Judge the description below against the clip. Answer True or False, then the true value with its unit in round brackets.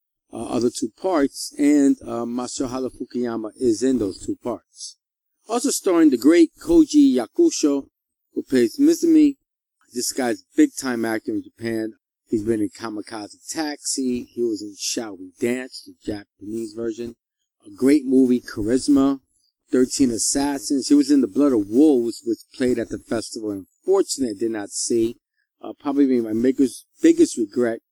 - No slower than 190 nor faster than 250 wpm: False (155 wpm)